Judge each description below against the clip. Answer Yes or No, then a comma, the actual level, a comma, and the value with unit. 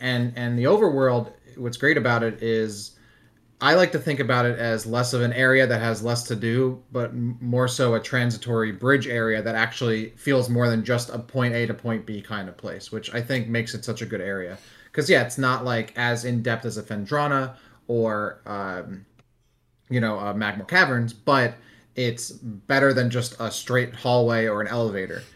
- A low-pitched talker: Yes, low, 120 Hz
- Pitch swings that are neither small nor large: No, narrow, 2.0 semitones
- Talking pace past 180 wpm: Yes, average, 200 wpm